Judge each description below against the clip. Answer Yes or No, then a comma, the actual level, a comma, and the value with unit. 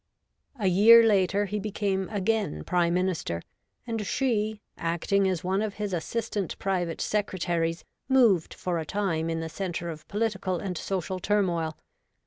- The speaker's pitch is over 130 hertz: Yes, high, 190 Hz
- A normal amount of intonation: Yes, average, 3.5 semitones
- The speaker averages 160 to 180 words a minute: No, average, 145 wpm